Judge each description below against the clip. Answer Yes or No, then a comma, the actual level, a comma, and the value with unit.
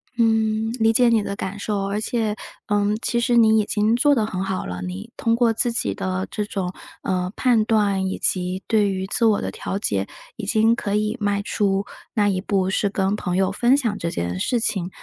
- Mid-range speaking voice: No, high, 205 Hz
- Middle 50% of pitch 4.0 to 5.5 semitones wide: No, average, 2.7 semitones